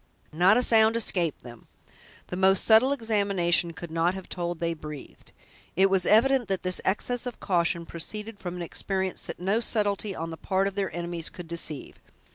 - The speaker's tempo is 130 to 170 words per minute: No, average, 185 wpm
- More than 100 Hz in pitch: Yes, high, 190 Hz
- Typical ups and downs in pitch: Yes, average, 3.7 semitones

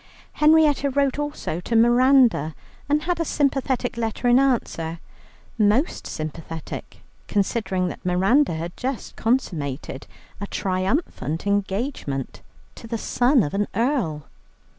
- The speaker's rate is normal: No, slow, 120 wpm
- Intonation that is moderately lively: No, wide, 7.4 semitones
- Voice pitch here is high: Yes, high, 230 Hz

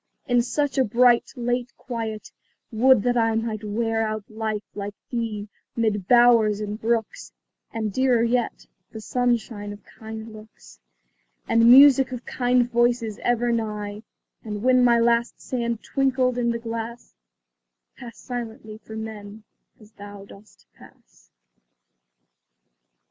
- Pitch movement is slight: Yes, narrow, 2.1 semitones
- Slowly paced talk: Yes, slow, 130 wpm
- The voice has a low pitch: No, high, 230 Hz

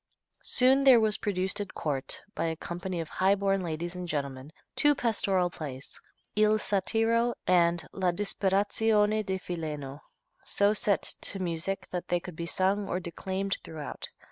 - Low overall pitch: No, high, 190 Hz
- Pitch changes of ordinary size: Yes, average, 3.5 semitones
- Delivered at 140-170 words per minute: Yes, average, 150 wpm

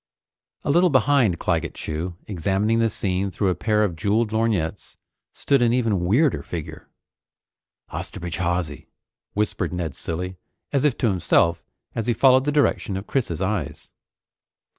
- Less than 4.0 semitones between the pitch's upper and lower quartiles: No, average, 5.1 semitones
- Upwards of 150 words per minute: No, average, 145 wpm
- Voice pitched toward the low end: Yes, low, 100 Hz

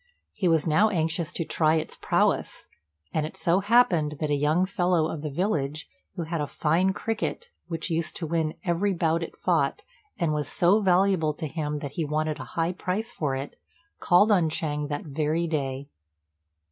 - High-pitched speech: No, medium, 160 Hz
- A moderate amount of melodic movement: Yes, average, 3.0 semitones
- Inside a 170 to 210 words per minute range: Yes, average, 185 wpm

